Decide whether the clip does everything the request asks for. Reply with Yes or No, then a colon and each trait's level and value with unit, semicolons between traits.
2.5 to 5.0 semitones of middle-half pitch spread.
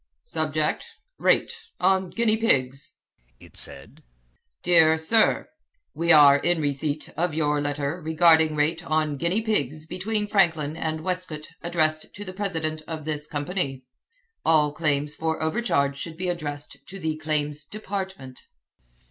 Yes: average, 3.1 semitones